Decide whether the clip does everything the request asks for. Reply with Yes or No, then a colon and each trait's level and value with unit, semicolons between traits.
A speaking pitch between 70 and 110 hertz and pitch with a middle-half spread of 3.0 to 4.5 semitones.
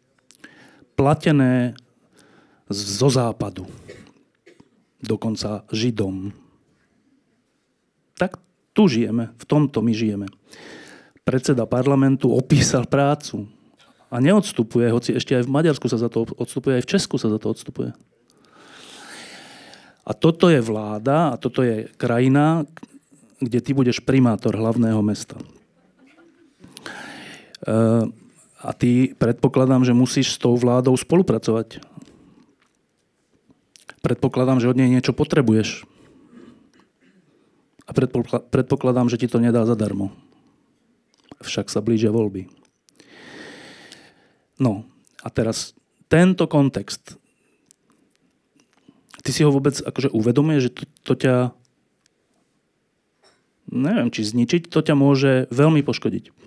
No: low, 125 Hz; average, 4.0 semitones